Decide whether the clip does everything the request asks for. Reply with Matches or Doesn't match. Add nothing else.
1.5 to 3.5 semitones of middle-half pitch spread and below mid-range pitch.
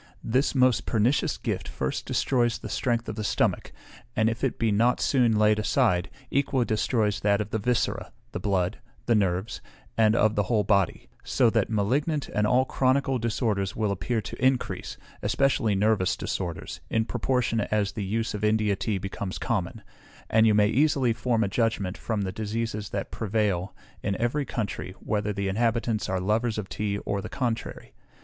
Matches